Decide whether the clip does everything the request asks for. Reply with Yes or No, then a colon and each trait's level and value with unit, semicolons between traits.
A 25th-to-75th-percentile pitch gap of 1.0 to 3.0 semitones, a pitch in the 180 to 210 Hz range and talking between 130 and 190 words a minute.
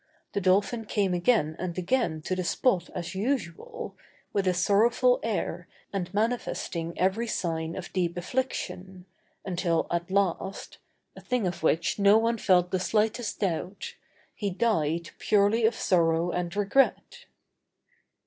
No: average, 4.0 semitones; high, 190 Hz; average, 140 wpm